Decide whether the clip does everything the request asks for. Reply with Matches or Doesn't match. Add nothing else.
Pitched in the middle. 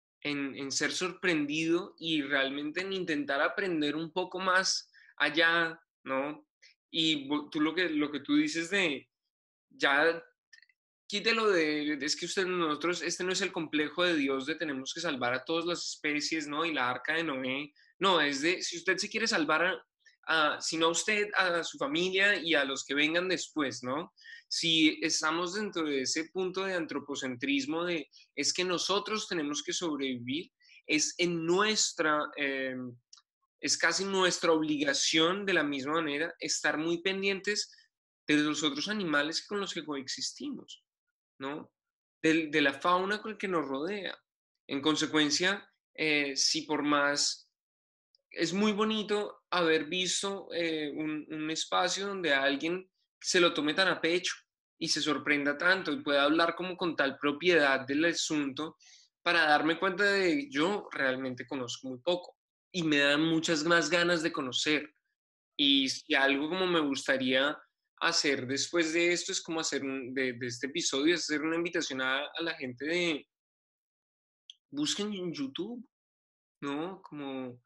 Matches